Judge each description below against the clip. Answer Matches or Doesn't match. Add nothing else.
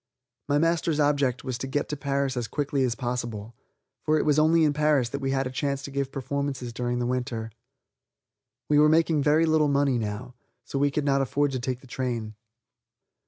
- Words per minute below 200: Doesn't match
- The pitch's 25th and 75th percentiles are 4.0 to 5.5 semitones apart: Doesn't match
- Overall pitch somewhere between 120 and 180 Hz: Matches